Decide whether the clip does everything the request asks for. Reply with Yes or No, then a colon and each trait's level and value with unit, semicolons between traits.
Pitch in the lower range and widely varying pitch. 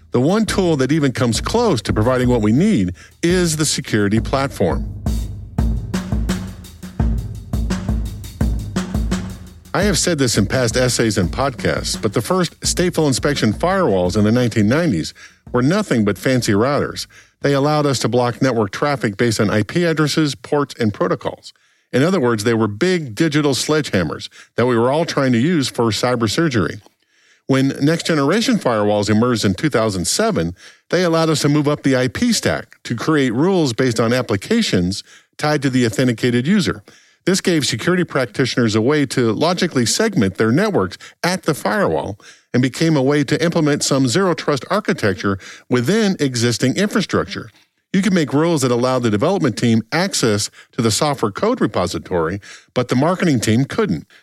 Yes: low, 130 Hz; wide, 6.2 semitones